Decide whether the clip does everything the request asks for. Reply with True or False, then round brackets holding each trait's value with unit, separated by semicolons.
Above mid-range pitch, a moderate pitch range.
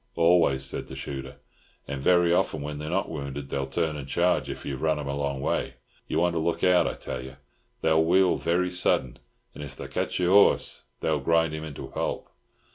False (80 Hz; 3.8 semitones)